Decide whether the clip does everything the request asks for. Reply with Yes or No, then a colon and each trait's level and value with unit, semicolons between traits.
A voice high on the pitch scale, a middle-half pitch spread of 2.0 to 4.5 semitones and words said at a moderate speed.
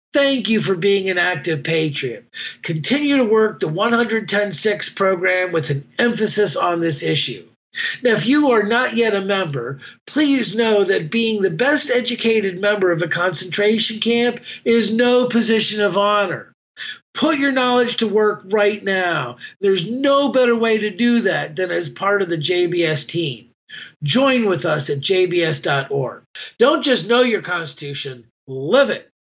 No: high, 205 Hz; average, 5.2 semitones; average, 160 wpm